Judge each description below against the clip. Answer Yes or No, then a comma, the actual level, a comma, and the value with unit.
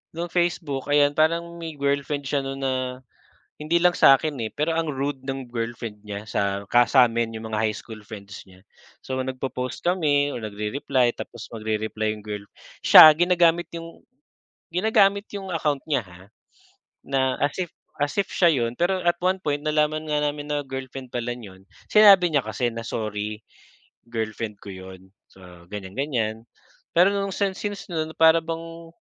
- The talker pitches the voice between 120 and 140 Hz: Yes, low, 135 Hz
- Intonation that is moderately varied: No, wide, 6.8 semitones